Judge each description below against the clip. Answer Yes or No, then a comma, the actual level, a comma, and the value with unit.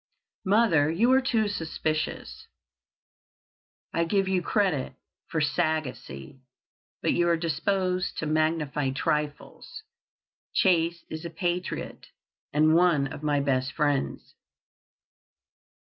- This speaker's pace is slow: Yes, slow, 105 wpm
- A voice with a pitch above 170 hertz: No, medium, 160 Hz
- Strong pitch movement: No, average, 3.4 semitones